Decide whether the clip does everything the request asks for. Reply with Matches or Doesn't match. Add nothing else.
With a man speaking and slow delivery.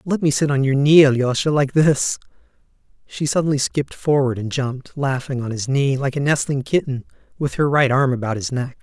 Doesn't match